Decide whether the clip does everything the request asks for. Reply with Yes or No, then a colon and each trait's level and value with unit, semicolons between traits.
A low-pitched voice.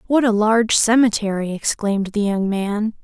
No: high, 210 Hz